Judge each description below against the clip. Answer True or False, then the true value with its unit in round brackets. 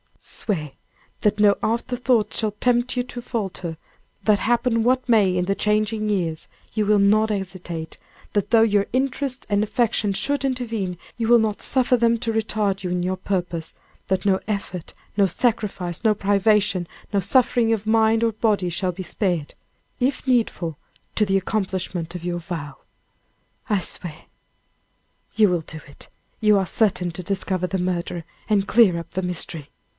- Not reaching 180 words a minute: True (165 wpm)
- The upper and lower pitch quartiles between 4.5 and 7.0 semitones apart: False (3.8 semitones)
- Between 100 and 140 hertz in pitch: False (205 Hz)